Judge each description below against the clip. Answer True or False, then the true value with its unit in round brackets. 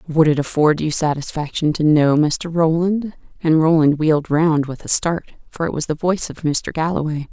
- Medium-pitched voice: True (155 Hz)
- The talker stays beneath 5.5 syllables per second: True (5.0 syllables/s)